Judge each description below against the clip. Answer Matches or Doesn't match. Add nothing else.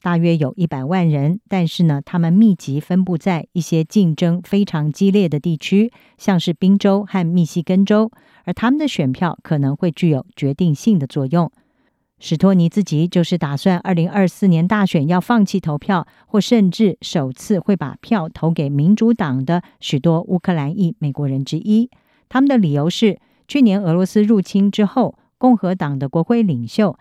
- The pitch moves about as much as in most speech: Matches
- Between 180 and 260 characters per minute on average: Doesn't match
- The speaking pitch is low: Doesn't match